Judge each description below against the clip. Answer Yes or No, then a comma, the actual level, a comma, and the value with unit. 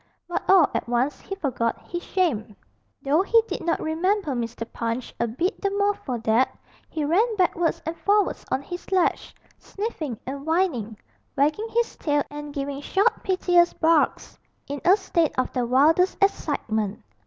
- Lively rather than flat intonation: Yes, wide, 6.5 semitones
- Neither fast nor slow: Yes, average, 165 wpm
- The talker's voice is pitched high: Yes, very high, 315 Hz